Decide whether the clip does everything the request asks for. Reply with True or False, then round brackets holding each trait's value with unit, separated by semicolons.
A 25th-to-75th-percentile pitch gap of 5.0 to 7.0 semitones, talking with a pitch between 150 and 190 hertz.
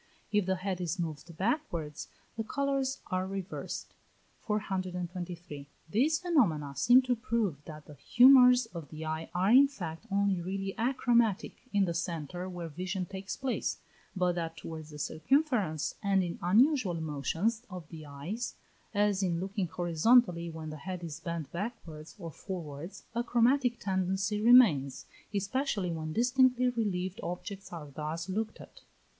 True (5.6 semitones; 185 Hz)